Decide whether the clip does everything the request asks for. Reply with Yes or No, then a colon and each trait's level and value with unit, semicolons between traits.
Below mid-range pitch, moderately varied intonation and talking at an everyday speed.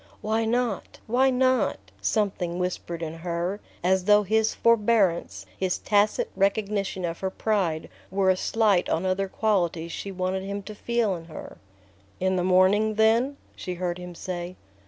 No: high, 190 Hz; average, 3.3 semitones; average, 155 wpm